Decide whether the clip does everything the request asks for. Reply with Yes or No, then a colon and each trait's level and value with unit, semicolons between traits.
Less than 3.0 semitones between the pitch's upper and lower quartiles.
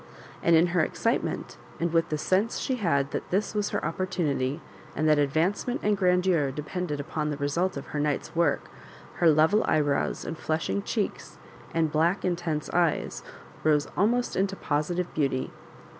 No: average, 3.5 semitones